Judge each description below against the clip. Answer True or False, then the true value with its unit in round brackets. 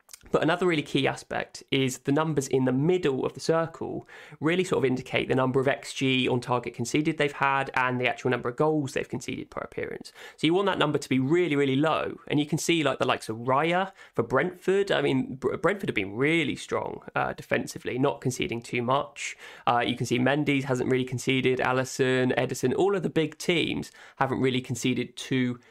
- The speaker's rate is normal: False (210 wpm)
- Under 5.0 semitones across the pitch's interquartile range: True (3.0 semitones)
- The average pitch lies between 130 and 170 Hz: True (135 Hz)